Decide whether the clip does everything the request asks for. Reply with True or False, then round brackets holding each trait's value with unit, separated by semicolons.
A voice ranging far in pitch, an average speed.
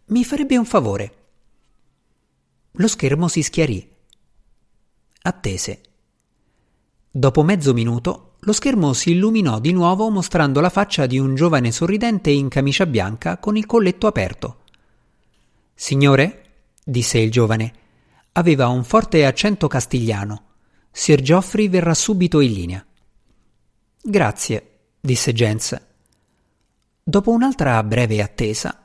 False (8.5 semitones; 110 wpm)